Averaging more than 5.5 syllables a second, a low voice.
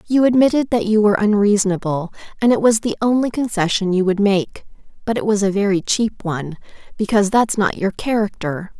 No: 5.8 syllables/s; high, 205 Hz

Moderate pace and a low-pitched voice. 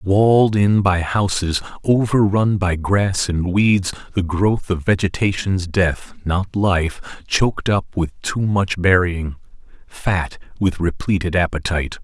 No: slow, 130 wpm; very low, 95 Hz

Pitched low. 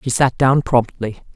Yes: low, 125 Hz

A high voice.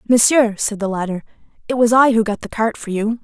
Yes: high, 220 Hz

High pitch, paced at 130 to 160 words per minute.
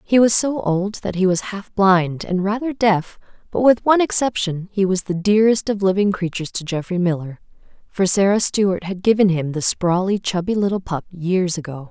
No: high, 195 Hz; average, 195 wpm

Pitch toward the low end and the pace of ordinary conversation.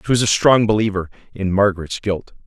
Yes: low, 100 Hz; average, 195 wpm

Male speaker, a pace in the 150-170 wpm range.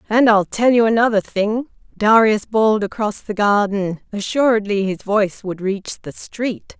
No: female; average, 160 wpm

